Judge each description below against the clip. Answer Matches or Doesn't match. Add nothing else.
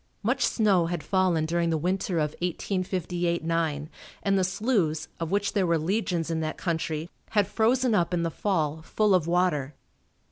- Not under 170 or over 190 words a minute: Matches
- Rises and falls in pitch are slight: Doesn't match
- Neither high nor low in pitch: Matches